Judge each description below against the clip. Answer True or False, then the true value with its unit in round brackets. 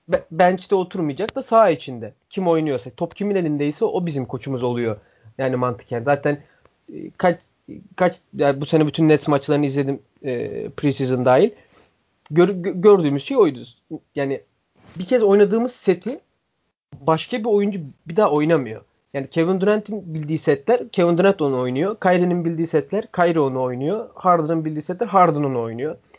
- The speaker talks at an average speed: False (155 wpm)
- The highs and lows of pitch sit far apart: False (5.0 semitones)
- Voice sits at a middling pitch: True (160 Hz)